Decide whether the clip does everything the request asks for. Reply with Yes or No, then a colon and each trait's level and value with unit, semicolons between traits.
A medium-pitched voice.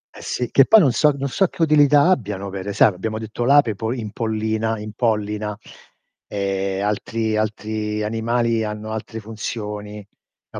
No: low, 110 Hz